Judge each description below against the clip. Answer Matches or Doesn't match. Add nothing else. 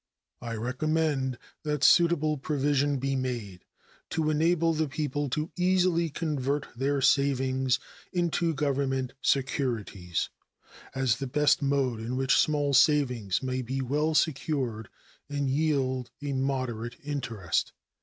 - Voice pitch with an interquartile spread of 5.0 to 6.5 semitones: Doesn't match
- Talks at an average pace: Doesn't match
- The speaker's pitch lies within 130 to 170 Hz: Matches